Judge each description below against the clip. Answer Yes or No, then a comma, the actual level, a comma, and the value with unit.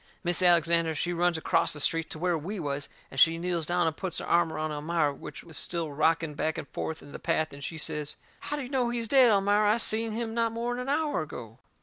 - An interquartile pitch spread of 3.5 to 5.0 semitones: No, wide, 5.6 semitones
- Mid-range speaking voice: Yes, medium, 170 Hz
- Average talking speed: No, fast, 250 wpm